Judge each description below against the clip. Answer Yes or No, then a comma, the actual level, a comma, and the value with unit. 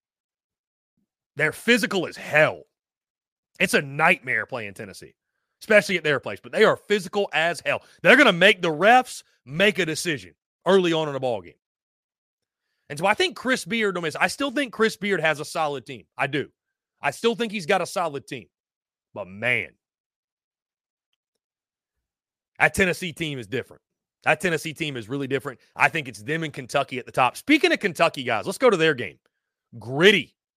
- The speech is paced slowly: No, average, 180 wpm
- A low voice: No, medium, 165 Hz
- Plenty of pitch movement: Yes, wide, 6.2 semitones